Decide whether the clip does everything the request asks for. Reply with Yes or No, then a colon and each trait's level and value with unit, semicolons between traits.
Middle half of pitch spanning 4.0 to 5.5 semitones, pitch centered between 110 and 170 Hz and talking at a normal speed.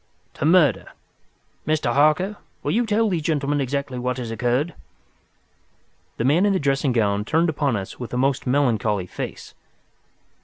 Yes: average, 4.4 semitones; medium, 140 Hz; average, 155 wpm